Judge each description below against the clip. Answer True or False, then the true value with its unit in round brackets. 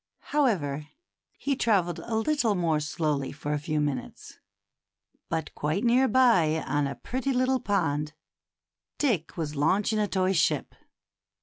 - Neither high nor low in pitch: True (175 Hz)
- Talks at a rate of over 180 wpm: False (135 wpm)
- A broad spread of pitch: True (7.8 semitones)